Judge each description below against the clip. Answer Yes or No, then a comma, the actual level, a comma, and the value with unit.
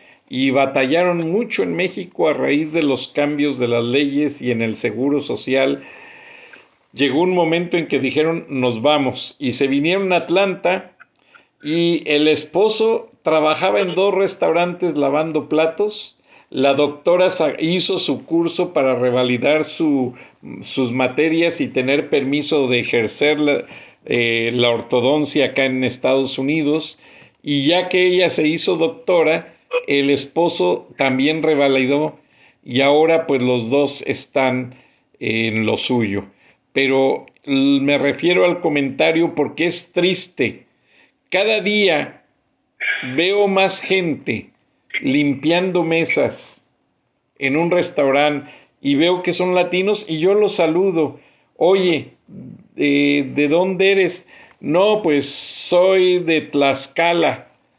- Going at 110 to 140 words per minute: Yes, slow, 125 wpm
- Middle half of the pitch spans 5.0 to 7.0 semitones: No, average, 4.5 semitones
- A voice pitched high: No, medium, 150 Hz